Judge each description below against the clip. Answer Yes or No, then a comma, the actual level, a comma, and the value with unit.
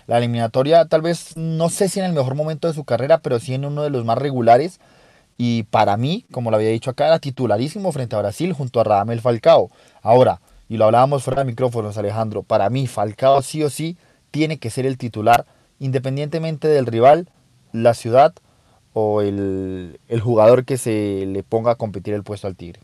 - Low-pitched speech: Yes, low, 125 Hz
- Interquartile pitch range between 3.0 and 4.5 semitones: No, average, 4.9 semitones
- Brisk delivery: Yes, fast, 200 wpm